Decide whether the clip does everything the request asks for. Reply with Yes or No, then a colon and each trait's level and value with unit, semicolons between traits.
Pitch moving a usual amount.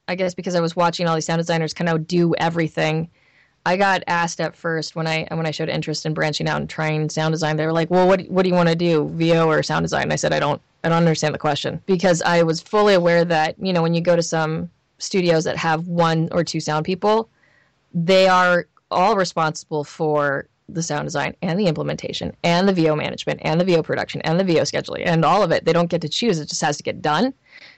No: narrow, 1.9 semitones